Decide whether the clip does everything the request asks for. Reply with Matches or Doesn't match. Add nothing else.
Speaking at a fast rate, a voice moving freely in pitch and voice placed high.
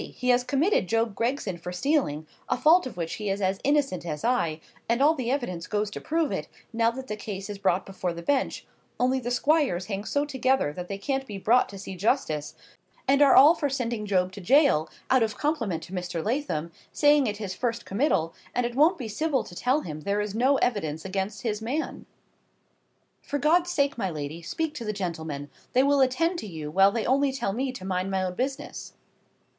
Matches